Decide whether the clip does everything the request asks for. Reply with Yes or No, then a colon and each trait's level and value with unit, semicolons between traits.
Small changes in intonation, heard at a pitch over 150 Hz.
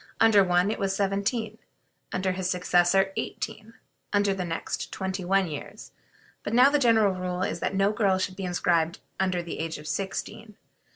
Yes: narrow, 2.2 semitones; high, 190 Hz